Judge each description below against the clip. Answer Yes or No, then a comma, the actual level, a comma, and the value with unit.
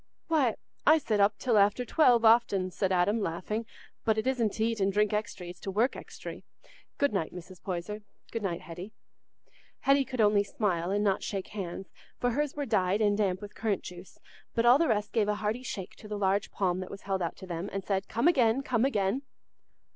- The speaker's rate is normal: No, fast, 215 wpm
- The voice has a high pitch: Yes, high, 210 Hz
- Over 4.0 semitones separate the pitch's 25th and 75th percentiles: No, average, 3.3 semitones